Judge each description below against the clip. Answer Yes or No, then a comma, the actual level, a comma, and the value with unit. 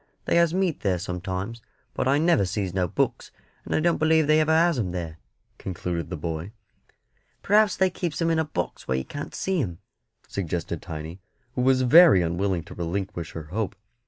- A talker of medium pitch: No, low, 100 Hz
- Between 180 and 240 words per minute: Yes, average, 190 wpm